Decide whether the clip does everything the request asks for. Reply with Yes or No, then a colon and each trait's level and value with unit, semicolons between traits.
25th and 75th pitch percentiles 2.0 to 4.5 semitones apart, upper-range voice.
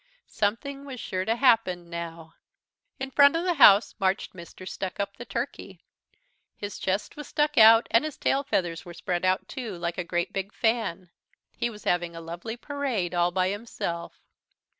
No: wide, 5.4 semitones; high, 200 Hz